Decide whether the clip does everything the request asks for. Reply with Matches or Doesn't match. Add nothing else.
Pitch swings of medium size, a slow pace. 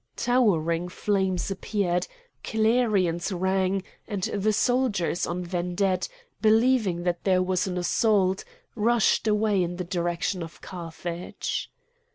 Matches